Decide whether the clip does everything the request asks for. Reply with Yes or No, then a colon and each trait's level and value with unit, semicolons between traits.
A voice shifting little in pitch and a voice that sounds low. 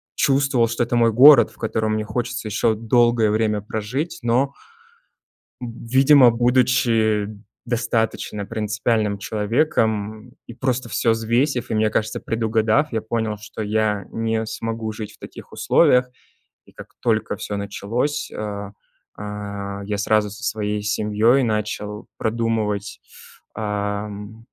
Yes: narrow, 2.1 semitones; low, 110 Hz